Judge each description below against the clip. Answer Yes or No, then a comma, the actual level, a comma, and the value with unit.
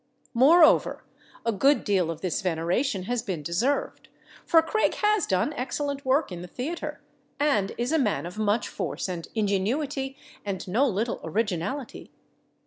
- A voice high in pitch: Yes, high, 230 Hz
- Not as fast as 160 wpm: Yes, average, 150 wpm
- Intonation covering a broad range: Yes, wide, 7.1 semitones